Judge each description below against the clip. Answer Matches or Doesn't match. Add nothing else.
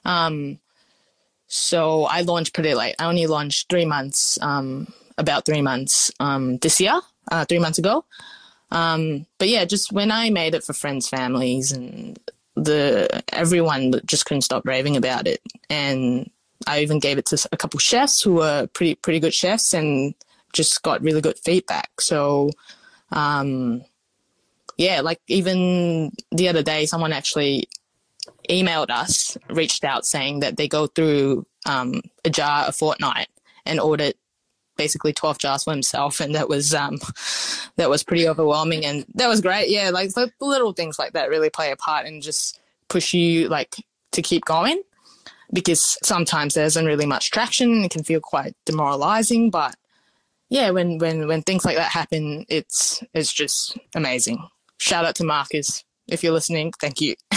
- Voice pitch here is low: Doesn't match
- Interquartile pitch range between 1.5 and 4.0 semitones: Matches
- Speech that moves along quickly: Doesn't match